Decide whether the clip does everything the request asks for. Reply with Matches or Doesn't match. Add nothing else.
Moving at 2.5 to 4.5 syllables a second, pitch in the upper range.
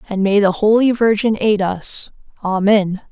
Matches